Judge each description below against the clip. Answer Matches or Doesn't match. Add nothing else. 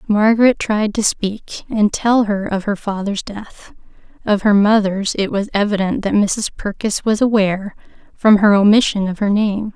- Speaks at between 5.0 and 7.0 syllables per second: Doesn't match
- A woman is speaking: Matches